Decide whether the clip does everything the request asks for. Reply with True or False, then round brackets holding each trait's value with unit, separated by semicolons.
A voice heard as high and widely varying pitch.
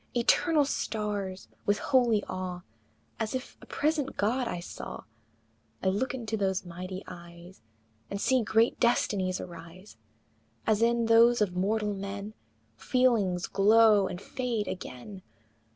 False (205 Hz; 3.9 semitones)